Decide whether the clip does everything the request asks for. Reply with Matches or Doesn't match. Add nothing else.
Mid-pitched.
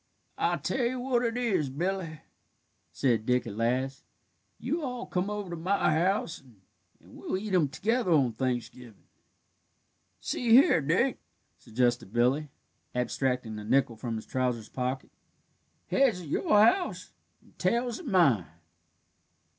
Matches